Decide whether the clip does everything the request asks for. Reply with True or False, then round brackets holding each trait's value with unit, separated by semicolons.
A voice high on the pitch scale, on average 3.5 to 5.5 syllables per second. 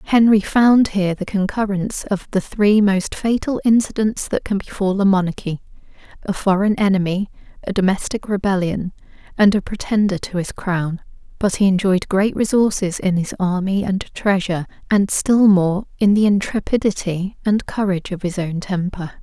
True (195 Hz; 5.0 syllables/s)